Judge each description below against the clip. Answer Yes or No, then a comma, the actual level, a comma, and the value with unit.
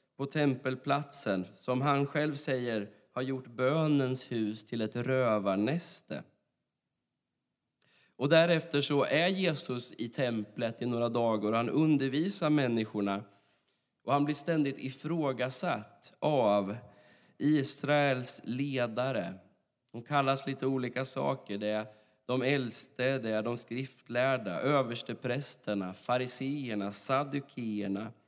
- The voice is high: No, low, 130 Hz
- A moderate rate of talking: No, slow, 110 wpm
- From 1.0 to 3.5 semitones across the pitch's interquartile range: No, average, 4.1 semitones